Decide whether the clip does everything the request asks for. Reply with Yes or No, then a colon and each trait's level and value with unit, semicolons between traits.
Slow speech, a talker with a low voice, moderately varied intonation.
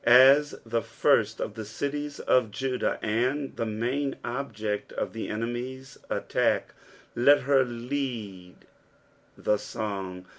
Yes: slow, 120 wpm; low, 120 Hz; average, 3.9 semitones